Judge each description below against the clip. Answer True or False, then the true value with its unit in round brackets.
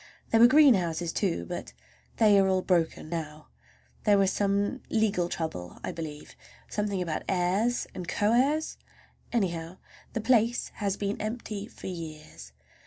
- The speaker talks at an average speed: True (150 wpm)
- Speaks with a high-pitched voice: True (195 Hz)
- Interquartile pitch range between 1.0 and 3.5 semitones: False (4.6 semitones)